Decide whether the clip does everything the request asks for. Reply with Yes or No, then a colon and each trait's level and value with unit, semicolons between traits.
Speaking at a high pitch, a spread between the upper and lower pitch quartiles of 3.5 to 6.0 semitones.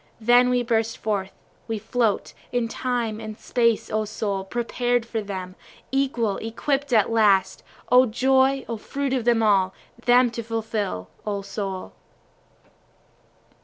No: high, 225 Hz; average, 2.7 semitones